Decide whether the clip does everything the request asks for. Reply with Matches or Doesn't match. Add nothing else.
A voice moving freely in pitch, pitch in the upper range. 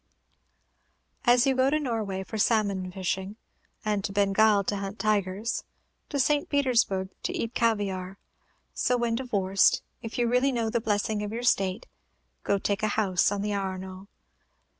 Doesn't match